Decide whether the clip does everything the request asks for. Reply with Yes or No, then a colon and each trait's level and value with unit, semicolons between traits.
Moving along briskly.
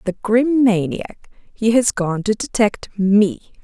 No: average, 150 wpm